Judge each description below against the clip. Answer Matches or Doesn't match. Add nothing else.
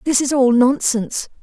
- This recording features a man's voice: Doesn't match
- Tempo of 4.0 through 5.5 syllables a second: Matches